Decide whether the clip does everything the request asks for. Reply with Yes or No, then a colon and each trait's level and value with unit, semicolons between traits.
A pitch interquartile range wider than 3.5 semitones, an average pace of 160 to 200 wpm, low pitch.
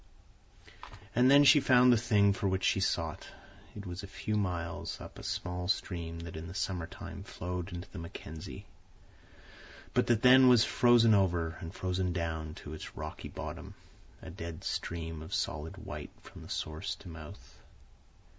Yes: average, 4.0 semitones; average, 165 wpm; very low, 90 Hz